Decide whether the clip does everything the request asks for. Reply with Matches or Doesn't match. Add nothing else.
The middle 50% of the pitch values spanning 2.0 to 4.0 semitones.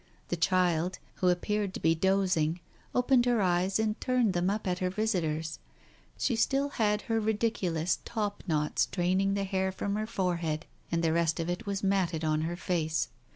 Matches